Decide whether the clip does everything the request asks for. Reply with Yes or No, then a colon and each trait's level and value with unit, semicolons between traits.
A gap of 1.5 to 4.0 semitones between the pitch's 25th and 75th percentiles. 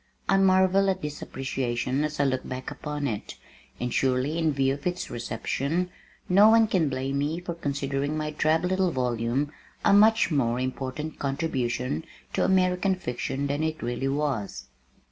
No: average, 4.9 semitones